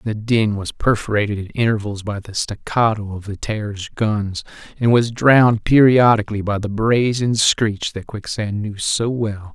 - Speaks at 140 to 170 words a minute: Yes, average, 165 wpm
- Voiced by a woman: No, male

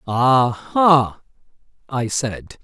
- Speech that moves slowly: Yes, slow, 70 wpm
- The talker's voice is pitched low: Yes, low, 130 Hz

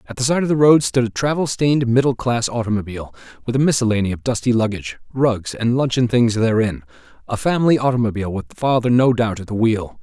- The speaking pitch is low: Yes, low, 115 Hz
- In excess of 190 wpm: Yes, average, 200 wpm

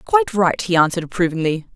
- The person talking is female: Yes, female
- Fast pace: No, average, 170 wpm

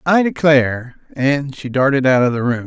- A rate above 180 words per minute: Yes, fast, 205 wpm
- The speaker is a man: Yes, male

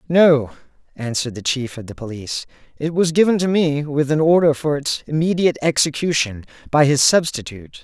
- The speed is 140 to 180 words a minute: Yes, average, 170 wpm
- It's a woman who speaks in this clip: No, male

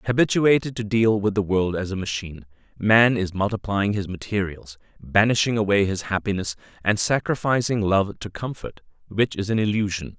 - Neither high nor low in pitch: No, low, 105 Hz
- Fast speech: No, average, 160 wpm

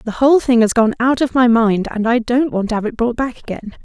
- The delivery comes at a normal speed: No, fast, 295 wpm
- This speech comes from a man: No, female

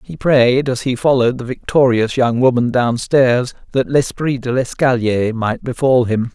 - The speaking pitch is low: Yes, low, 125 Hz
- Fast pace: No, average, 160 wpm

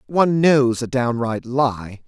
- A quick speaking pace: No, average, 145 wpm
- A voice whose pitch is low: Yes, low, 125 Hz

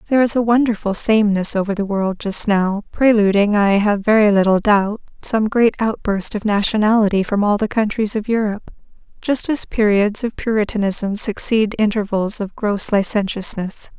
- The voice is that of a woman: Yes, female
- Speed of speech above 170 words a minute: No, average, 155 wpm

